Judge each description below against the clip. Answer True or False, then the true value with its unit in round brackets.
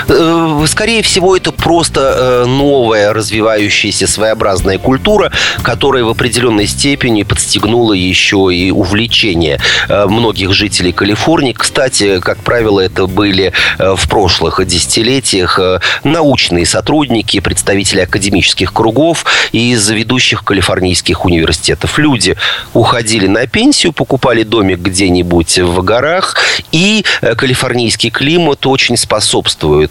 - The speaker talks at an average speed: False (100 wpm)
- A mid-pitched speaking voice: False (110 Hz)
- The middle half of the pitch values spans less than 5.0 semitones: False (5.4 semitones)